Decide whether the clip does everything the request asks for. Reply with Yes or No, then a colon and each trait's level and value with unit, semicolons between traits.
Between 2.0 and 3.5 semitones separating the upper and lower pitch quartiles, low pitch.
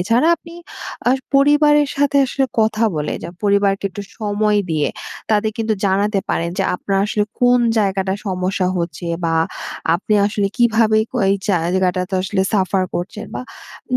No: average, 3.1 semitones; high, 205 Hz